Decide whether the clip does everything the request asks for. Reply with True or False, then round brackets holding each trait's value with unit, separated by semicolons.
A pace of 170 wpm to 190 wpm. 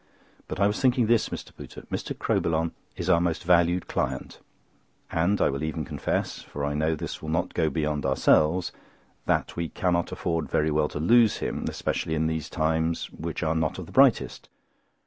True (180 wpm)